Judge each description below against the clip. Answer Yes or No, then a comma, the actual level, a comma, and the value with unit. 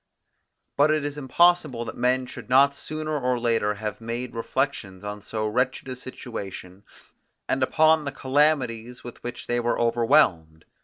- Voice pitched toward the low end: Yes, low, 125 Hz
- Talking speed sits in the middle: Yes, average, 155 wpm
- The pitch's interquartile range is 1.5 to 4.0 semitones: Yes, average, 3.7 semitones